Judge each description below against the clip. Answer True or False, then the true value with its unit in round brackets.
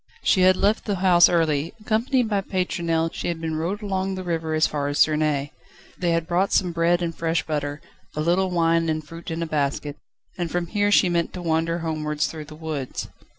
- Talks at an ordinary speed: False (210 wpm)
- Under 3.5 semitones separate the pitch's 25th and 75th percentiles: True (2.7 semitones)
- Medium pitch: True (165 Hz)